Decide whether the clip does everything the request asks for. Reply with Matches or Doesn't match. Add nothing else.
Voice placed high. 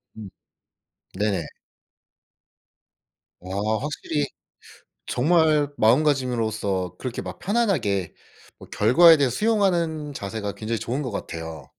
Doesn't match